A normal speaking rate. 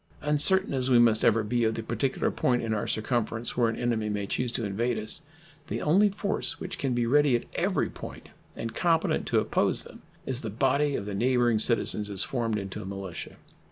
No: fast, 210 wpm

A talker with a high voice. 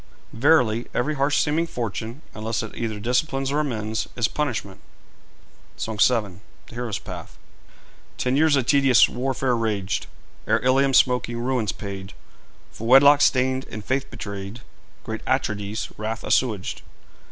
No: low, 120 Hz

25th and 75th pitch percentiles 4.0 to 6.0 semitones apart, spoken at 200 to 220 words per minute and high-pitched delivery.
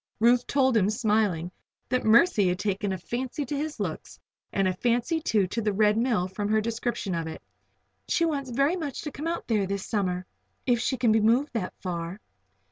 Yes: average, 4.8 semitones; fast, 205 wpm; high, 220 Hz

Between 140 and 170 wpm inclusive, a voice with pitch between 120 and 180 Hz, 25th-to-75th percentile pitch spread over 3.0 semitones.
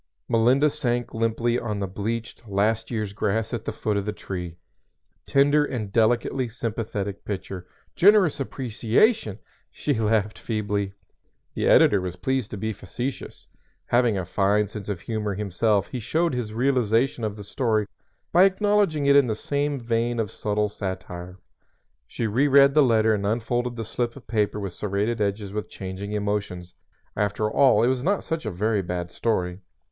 No: average, 165 wpm; low, 110 Hz; average, 3.4 semitones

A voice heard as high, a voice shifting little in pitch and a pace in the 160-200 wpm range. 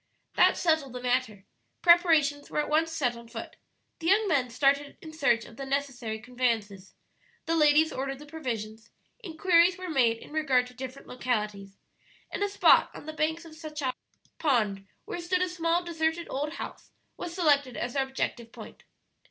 No: very high, 285 Hz; average, 4.8 semitones; average, 175 wpm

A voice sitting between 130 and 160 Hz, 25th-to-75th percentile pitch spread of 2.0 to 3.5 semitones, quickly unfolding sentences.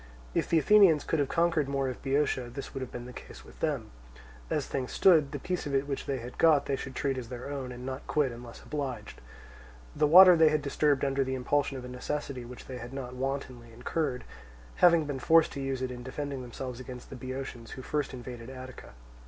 Yes: low, 135 Hz; narrow, 2.6 semitones; fast, 225 wpm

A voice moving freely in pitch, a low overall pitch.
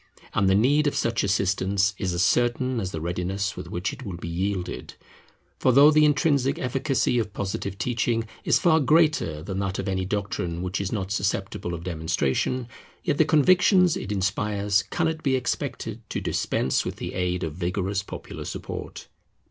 Yes: wide, 5.8 semitones; low, 100 Hz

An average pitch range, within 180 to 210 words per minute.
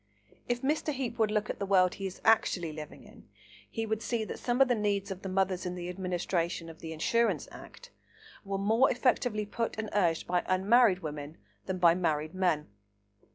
Yes: average, 4.2 semitones; average, 200 wpm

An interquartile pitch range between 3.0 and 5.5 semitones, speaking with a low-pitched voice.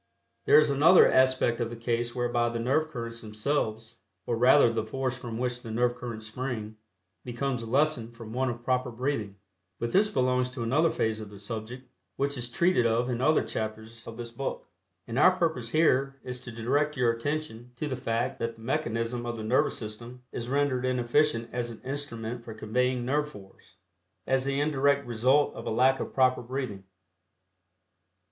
No: narrow, 2.6 semitones; low, 120 Hz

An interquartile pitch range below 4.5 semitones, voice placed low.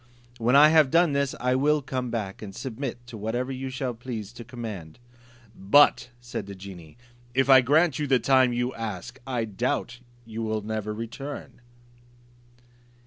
Yes: average, 3.4 semitones; low, 120 Hz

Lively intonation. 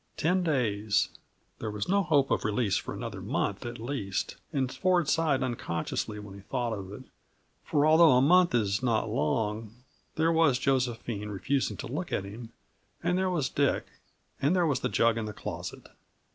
Yes: wide, 6.5 semitones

